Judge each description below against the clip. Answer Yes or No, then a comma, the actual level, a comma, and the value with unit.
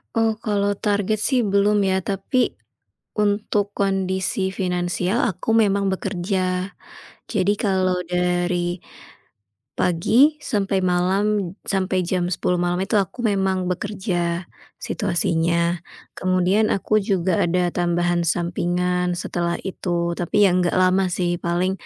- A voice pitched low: No, medium, 185 Hz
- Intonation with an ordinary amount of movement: No, narrow, 2.2 semitones